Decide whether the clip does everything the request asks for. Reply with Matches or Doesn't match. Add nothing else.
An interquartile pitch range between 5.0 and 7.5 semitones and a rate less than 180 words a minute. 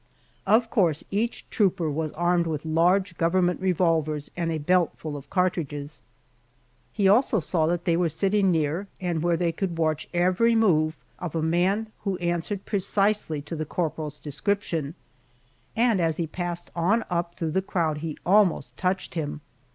Doesn't match